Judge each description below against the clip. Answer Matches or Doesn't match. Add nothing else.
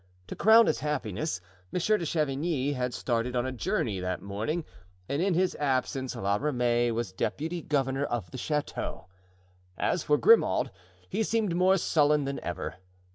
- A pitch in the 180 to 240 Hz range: Doesn't match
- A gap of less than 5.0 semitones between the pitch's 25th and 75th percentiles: Doesn't match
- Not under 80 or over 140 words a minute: Doesn't match